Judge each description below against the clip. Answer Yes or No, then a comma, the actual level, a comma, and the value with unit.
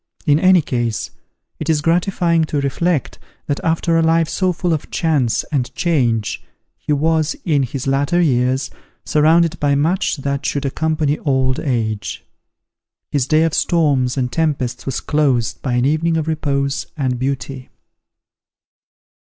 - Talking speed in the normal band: Yes, average, 145 wpm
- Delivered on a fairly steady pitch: No, average, 3.5 semitones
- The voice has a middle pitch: Yes, medium, 145 Hz